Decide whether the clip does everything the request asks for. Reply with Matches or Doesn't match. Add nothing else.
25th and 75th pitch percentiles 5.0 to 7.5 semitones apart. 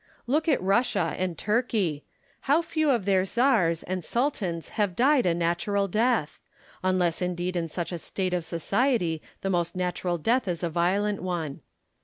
Matches